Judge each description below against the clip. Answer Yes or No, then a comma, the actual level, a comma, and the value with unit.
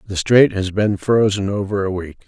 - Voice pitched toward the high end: No, low, 100 Hz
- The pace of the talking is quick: Yes, fast, 210 wpm